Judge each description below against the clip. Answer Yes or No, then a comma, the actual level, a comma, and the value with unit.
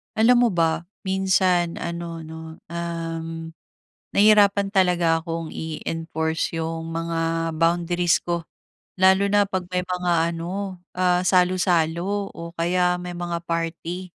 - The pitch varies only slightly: Yes, narrow, 1.9 semitones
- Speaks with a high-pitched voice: No, medium, 170 Hz